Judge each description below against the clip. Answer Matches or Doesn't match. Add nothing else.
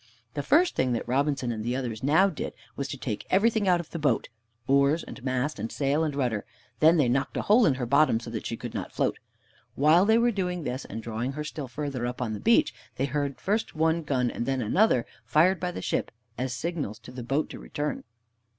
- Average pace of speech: Doesn't match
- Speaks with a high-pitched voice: Doesn't match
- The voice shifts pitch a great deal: Doesn't match